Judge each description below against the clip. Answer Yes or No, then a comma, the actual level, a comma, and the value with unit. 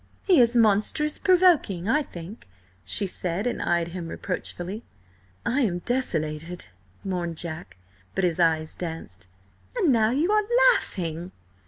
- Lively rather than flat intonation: Yes, wide, 7.4 semitones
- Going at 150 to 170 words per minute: No, slow, 135 wpm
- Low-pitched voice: No, medium, 185 Hz